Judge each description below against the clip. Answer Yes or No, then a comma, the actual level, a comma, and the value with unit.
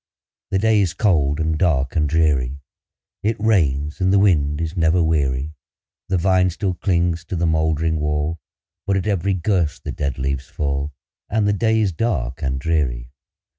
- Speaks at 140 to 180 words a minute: Yes, average, 170 wpm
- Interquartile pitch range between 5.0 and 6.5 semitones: No, average, 4.5 semitones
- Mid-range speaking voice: No, very low, 80 Hz